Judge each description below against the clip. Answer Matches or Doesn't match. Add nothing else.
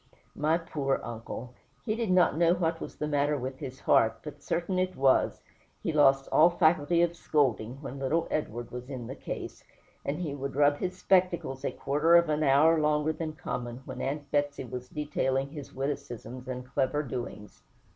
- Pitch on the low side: Doesn't match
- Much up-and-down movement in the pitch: Doesn't match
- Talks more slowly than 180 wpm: Doesn't match